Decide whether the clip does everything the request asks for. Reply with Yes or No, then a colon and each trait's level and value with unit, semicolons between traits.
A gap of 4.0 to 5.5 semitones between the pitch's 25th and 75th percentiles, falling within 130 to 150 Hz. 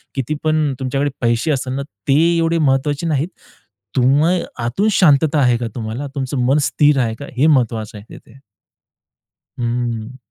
No: average, 3.5 semitones; low, 135 Hz